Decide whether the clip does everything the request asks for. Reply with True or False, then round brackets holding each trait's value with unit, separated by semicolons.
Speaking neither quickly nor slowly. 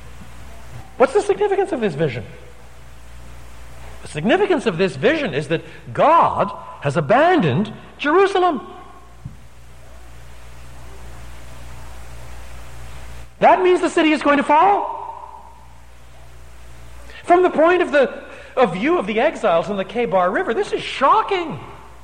False (115 wpm)